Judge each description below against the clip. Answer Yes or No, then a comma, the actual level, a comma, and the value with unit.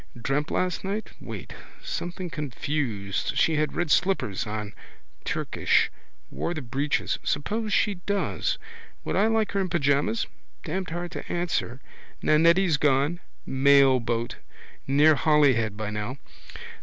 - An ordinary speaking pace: No, slow, 125 wpm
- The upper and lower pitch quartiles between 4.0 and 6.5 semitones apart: Yes, average, 5.2 semitones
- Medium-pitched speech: Yes, medium, 150 Hz